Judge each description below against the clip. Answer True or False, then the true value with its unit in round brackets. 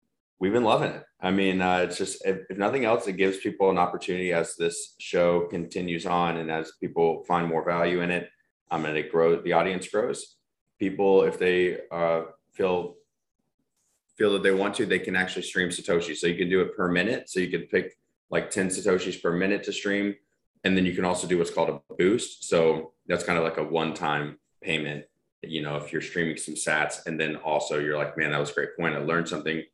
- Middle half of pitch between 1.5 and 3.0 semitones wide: True (2.6 semitones)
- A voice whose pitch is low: True (85 Hz)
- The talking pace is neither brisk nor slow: False (225 wpm)